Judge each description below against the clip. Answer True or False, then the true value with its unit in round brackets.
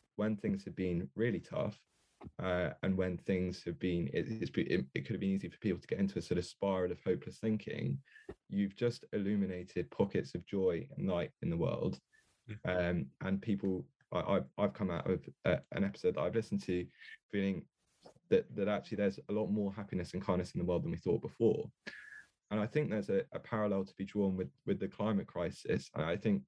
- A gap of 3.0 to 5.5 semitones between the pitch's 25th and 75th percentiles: False (2.4 semitones)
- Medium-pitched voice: False (100 Hz)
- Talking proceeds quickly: True (210 wpm)